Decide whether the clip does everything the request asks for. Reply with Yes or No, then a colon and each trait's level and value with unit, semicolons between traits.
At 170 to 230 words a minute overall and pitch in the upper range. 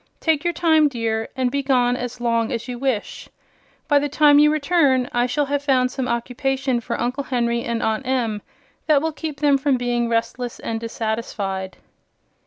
Yes: average, 185 wpm; very high, 255 Hz